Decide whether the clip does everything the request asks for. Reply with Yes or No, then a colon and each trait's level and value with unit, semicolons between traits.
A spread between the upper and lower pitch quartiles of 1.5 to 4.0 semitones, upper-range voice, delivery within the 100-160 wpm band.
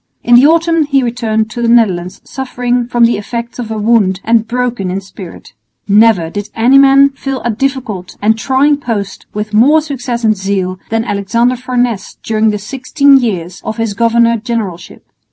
No: average, 3.2 semitones; high, 230 Hz; average, 175 wpm